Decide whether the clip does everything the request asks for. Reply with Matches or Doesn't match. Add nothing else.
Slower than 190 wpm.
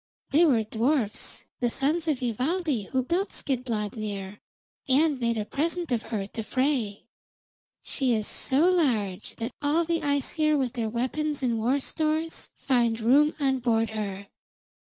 Matches